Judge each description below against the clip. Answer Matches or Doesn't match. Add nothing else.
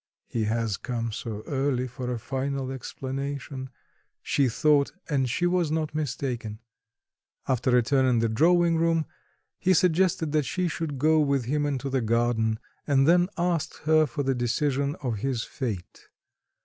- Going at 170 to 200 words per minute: Doesn't match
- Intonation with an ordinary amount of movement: Matches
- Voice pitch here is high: Doesn't match